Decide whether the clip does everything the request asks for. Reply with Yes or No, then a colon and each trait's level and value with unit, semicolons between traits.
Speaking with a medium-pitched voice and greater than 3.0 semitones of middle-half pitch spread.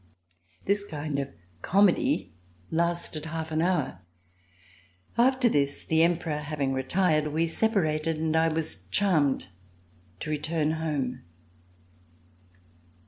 No: medium, 160 Hz; narrow, 2.4 semitones